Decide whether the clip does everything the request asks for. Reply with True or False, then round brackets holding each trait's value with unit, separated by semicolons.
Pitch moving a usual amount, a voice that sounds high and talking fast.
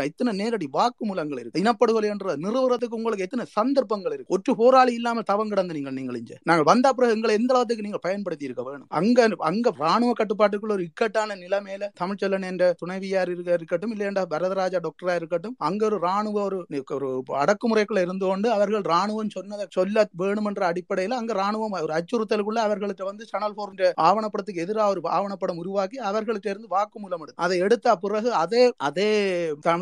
True (3.6 semitones; 205 Hz; 165 wpm)